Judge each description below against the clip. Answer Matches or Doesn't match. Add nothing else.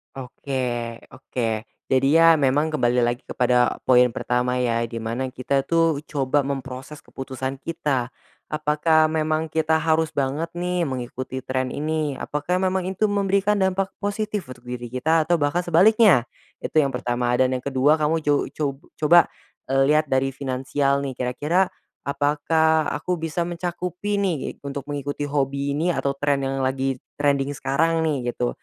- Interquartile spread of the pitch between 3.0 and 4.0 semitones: Matches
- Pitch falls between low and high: Matches